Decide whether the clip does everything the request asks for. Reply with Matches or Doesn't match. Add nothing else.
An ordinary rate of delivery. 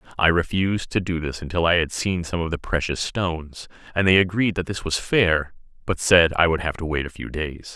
Doesn't match